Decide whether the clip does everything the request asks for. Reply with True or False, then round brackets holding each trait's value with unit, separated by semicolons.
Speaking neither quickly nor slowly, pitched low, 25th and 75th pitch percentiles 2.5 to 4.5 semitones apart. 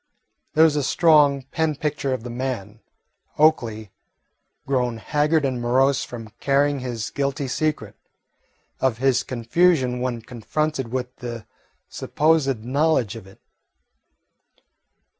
False (120 wpm; 130 Hz; 3.7 semitones)